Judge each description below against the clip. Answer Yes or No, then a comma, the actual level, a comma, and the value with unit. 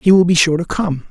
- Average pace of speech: No, fast, 325 wpm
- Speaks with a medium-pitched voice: Yes, medium, 170 Hz